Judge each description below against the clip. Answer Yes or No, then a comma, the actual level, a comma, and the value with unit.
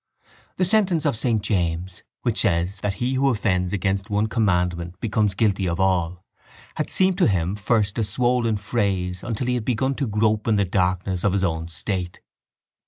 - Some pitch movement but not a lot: Yes, average, 4.1 semitones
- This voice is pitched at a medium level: No, low, 100 Hz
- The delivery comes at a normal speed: Yes, average, 180 wpm